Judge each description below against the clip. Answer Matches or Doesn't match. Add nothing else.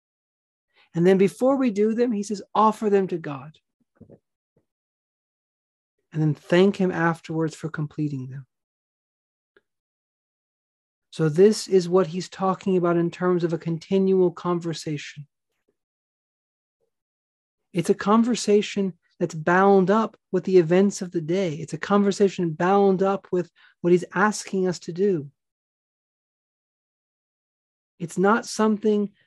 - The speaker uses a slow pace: Matches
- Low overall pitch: Doesn't match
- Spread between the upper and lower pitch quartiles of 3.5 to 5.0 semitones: Doesn't match